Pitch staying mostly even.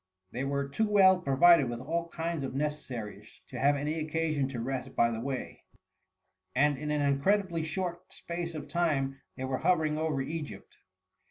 No: average, 3.6 semitones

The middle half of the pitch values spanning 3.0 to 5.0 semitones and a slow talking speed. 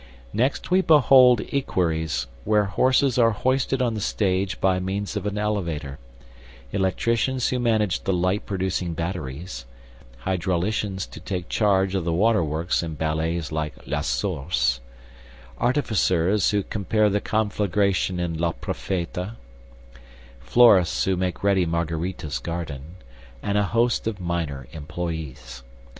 Yes: average, 4.3 semitones; slow, 130 wpm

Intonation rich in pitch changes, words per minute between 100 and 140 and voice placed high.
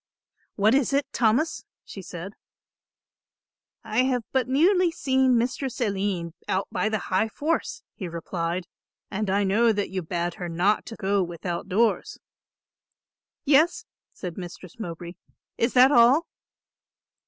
Yes: wide, 5.9 semitones; slow, 135 wpm; high, 210 Hz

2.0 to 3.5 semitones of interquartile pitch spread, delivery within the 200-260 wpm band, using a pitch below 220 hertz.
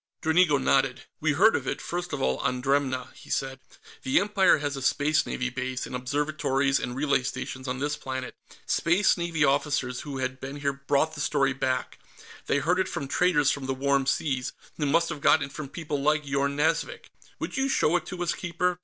Yes: average, 3.1 semitones; fast, 205 wpm; medium, 140 Hz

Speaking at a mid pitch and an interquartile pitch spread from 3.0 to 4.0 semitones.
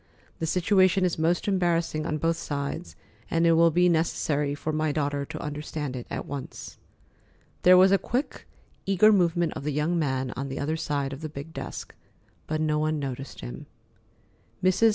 Yes: medium, 155 Hz; average, 3.3 semitones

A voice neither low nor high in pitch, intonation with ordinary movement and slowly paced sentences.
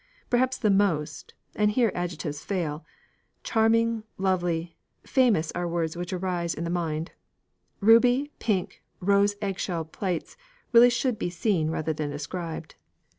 Yes: medium, 180 Hz; average, 4.8 semitones; slow, 130 wpm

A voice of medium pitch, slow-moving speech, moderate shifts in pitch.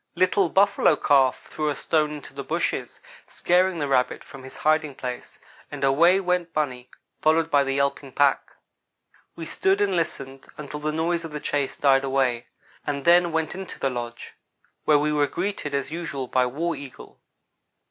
No: medium, 150 Hz; average, 175 wpm; average, 3.7 semitones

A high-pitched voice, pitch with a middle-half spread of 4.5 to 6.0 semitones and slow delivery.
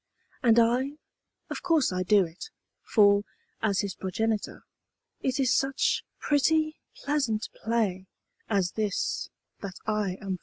Yes: high, 220 Hz; average, 5.1 semitones; slow, 130 wpm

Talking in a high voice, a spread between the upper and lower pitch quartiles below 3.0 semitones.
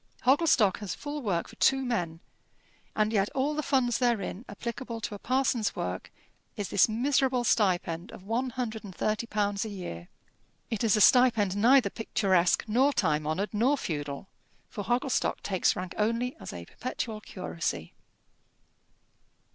No: high, 215 Hz; average, 4.7 semitones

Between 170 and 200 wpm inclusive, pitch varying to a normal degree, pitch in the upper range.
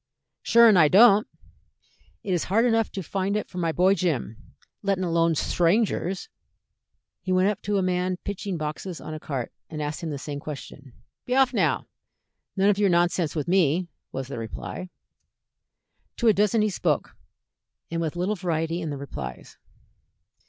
No: average, 175 wpm; average, 4.2 semitones; medium, 180 Hz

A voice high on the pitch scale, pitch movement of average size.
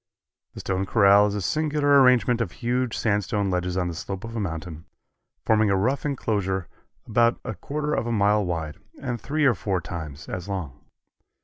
No: low, 105 Hz; average, 5.0 semitones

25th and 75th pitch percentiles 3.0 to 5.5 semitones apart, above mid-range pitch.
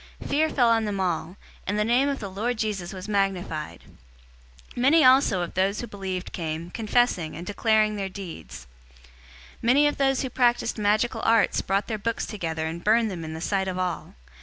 Yes: average, 4.4 semitones; high, 205 Hz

